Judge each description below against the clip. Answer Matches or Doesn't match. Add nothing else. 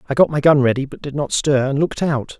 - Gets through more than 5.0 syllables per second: Matches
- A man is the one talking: Matches